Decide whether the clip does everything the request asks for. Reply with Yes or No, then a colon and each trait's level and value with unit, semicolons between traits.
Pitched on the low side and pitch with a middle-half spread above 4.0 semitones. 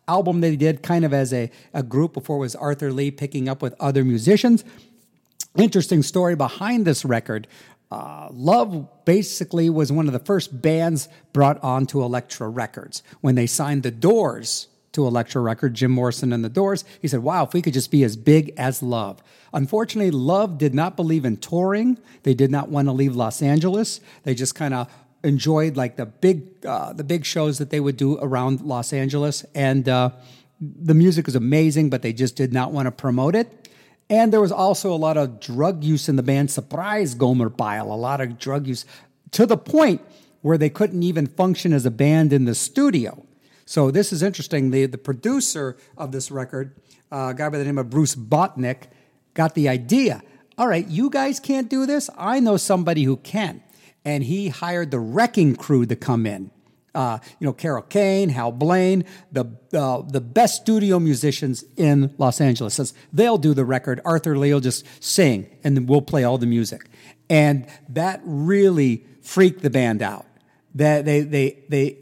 No: medium, 145 Hz; average, 5.1 semitones